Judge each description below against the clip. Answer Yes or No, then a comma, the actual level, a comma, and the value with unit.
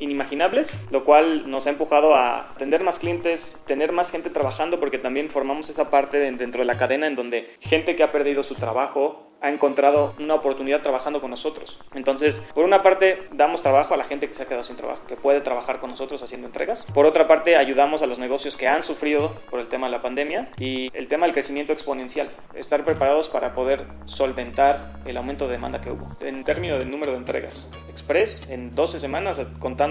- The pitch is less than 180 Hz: Yes, medium, 140 Hz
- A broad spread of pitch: No, average, 2.9 semitones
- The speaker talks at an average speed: No, fast, 210 wpm